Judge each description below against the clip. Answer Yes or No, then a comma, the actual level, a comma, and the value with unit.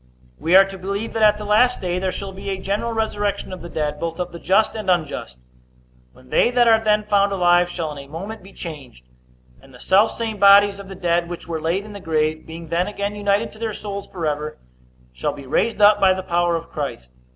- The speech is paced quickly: Yes, fast, 230 wpm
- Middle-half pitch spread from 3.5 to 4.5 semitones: Yes, average, 3.8 semitones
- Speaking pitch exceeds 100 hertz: Yes, high, 190 Hz